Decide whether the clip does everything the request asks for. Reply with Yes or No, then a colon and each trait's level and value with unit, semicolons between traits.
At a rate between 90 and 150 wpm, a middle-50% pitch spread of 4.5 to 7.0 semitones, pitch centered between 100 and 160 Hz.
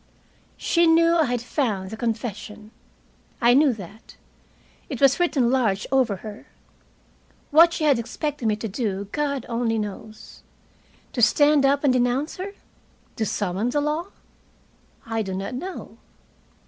No: average, 145 wpm; average, 5.2 semitones; high, 245 Hz